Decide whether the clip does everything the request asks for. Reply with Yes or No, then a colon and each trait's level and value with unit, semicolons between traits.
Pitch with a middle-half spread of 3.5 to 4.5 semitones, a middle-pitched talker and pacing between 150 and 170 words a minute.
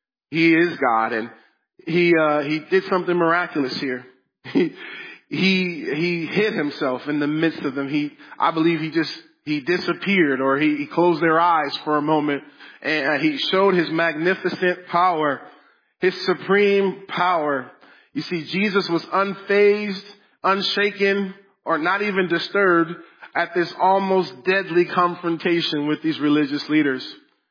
No: average, 3.9 semitones; medium, 175 Hz; average, 140 wpm